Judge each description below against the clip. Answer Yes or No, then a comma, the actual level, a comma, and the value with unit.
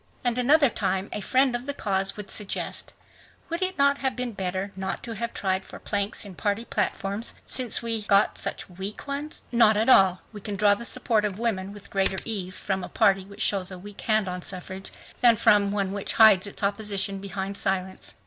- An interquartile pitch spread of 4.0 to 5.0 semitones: No, average, 3.1 semitones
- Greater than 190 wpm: Yes, fast, 205 wpm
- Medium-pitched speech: No, high, 205 Hz